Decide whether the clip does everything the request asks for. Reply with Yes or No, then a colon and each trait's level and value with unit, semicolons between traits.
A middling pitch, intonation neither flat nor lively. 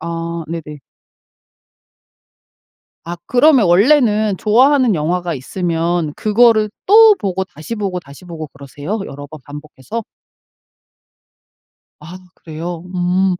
Yes: medium, 175 Hz; average, 5.0 semitones